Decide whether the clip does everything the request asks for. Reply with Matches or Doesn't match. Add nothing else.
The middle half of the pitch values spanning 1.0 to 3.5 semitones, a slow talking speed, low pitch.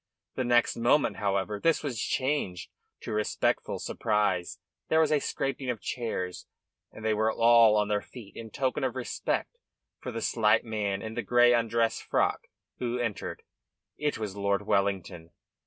Doesn't match